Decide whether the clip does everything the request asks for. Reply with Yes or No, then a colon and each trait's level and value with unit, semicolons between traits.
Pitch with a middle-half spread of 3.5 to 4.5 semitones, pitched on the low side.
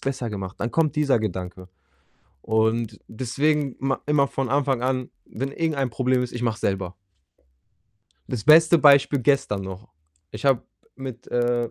Yes: average, 3.8 semitones; low, 125 Hz